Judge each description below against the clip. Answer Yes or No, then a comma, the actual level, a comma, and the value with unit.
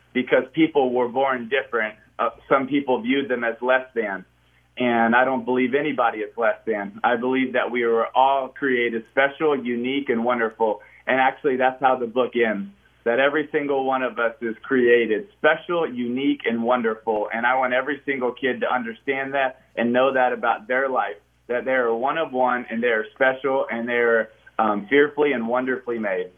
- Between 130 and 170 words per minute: No, average, 190 wpm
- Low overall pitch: Yes, low, 125 Hz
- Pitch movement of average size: No, narrow, 2.3 semitones